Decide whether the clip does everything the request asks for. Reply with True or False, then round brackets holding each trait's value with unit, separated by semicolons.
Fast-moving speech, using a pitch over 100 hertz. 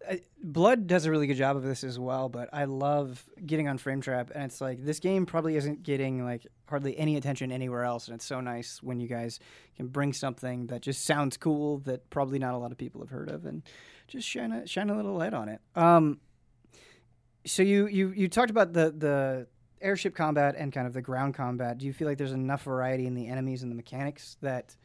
True (230 wpm; 135 Hz)